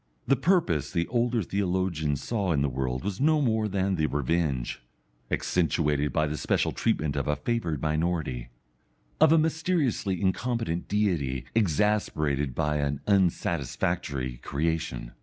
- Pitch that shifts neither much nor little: No, wide, 6.5 semitones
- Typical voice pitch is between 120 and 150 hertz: No, very low, 85 Hz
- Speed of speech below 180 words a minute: Yes, slow, 135 wpm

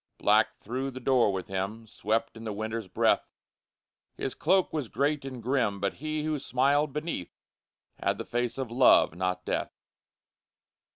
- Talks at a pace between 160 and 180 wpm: Yes, average, 165 wpm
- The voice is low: Yes, low, 120 Hz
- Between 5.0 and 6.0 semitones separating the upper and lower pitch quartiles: No, average, 4.6 semitones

